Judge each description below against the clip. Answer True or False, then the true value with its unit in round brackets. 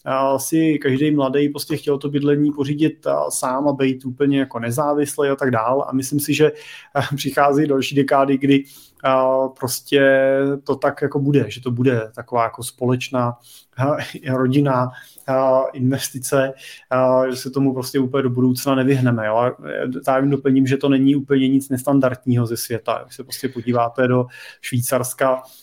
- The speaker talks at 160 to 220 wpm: True (165 wpm)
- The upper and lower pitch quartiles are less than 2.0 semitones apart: True (1.6 semitones)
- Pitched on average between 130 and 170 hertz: True (135 Hz)